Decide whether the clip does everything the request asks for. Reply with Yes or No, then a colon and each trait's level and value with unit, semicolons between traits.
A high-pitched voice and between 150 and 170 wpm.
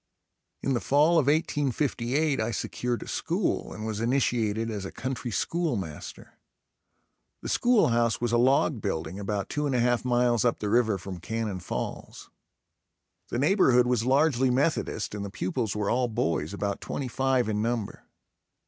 No: low, 120 Hz; average, 165 wpm